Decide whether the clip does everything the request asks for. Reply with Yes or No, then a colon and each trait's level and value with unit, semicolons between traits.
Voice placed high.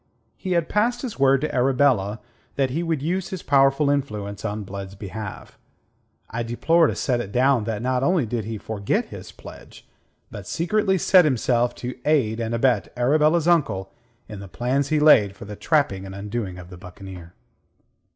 No: low, 125 Hz